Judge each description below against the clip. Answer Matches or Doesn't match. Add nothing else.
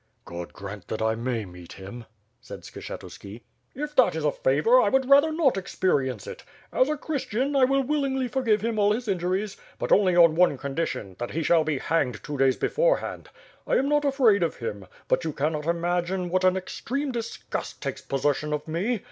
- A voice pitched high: Doesn't match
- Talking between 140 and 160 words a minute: Doesn't match